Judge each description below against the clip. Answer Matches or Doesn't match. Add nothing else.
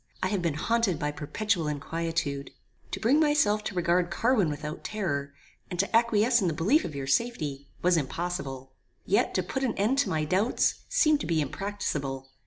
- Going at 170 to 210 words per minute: Matches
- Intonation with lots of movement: Matches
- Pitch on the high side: Doesn't match